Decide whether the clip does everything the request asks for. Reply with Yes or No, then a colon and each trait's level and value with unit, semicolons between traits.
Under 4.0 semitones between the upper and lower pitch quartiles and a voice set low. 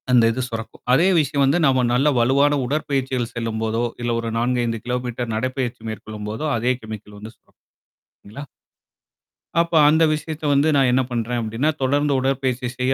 Yes: average, 3.3 semitones; low, 125 Hz